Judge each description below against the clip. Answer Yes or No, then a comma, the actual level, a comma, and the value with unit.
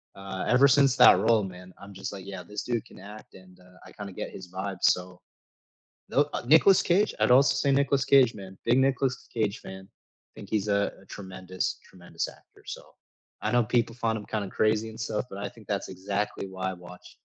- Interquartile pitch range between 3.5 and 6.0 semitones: Yes, average, 4.3 semitones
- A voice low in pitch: Yes, low, 105 Hz